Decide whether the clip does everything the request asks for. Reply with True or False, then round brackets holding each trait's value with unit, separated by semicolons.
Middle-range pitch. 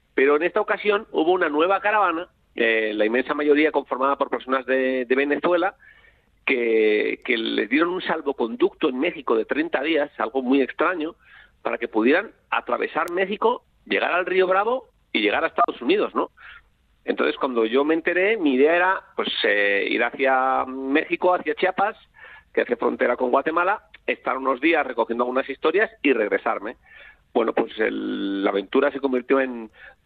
True (155 Hz)